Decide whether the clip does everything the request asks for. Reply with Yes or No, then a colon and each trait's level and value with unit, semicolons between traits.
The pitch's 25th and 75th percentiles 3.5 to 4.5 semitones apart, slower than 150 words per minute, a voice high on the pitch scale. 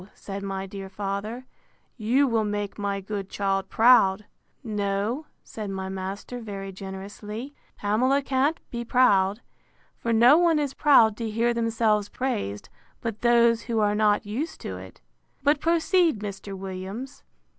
Yes: average, 3.8 semitones; average, 140 wpm; high, 215 Hz